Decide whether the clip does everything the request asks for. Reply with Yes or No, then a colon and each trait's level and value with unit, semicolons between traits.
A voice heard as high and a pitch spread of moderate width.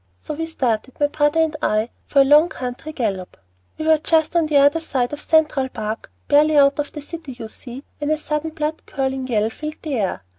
Yes: very high, 290 Hz; average, 3.6 semitones